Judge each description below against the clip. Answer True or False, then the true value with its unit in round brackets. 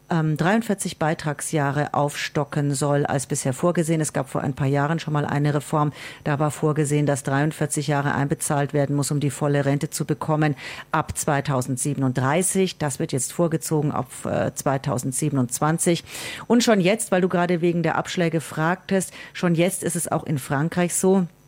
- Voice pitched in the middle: True (150 Hz)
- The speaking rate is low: False (160 wpm)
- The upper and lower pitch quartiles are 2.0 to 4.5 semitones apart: True (2.9 semitones)